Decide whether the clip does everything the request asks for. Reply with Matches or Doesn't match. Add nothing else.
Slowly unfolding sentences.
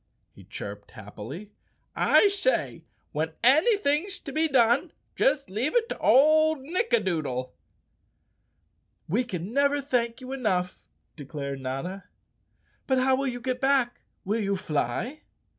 Matches